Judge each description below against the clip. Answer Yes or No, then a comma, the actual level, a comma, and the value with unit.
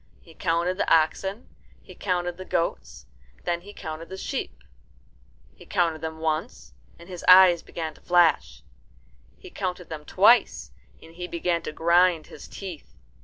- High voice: No, medium, 170 Hz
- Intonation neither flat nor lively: No, narrow, 2.3 semitones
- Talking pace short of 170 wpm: Yes, average, 160 wpm